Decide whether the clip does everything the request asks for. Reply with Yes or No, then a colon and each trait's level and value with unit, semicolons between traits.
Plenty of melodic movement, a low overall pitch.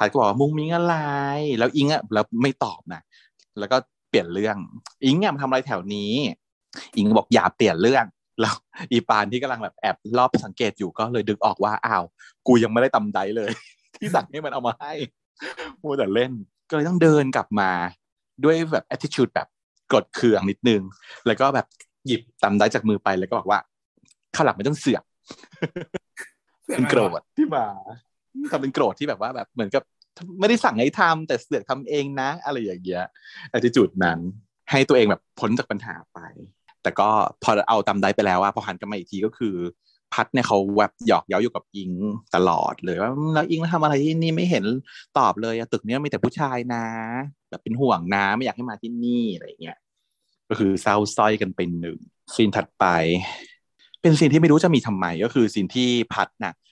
Yes: wide, 6.5 semitones; low, 125 Hz